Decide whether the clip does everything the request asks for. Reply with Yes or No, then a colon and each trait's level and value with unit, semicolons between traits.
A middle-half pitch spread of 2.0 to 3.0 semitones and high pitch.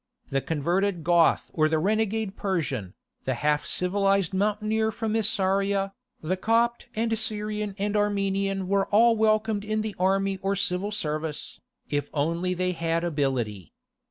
No: average, 4.1 semitones; high, 195 Hz